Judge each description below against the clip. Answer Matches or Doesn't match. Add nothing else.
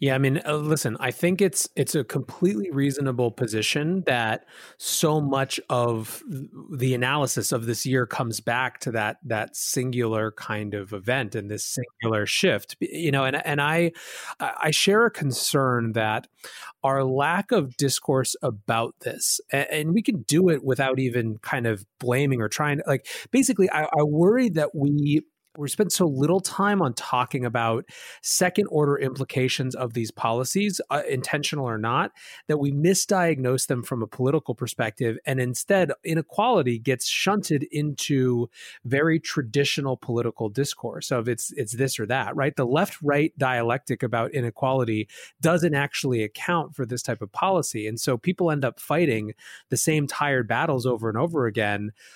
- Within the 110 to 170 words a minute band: Matches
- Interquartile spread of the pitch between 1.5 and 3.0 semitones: Doesn't match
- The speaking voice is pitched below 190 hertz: Matches